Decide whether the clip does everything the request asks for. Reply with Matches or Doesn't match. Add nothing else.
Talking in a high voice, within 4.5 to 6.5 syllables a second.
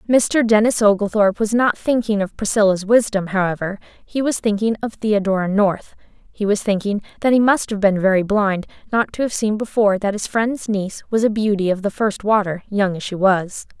Matches